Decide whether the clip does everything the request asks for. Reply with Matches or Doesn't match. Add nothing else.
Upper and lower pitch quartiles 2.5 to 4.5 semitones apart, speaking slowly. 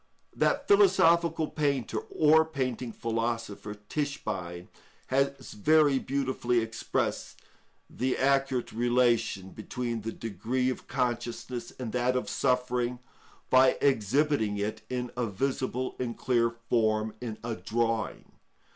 Matches